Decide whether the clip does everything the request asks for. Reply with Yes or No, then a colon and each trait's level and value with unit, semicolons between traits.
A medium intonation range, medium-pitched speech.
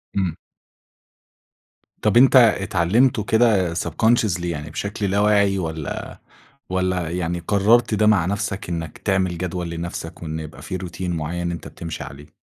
No: average, 3.5 semitones; very low, 90 Hz